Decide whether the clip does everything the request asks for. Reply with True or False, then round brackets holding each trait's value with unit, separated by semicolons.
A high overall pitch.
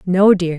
False (180 Hz)